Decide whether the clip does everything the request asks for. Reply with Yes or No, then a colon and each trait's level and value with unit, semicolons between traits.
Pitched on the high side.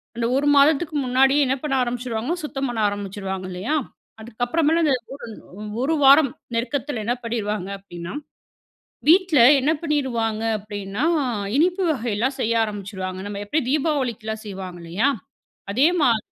Yes: high, 240 Hz